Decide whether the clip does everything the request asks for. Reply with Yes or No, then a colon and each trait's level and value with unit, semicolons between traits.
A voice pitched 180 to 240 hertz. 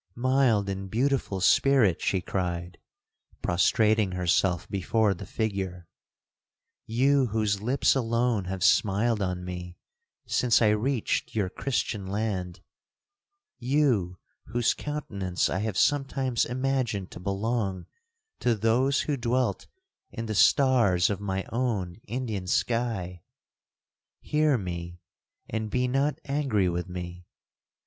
No: low, 110 Hz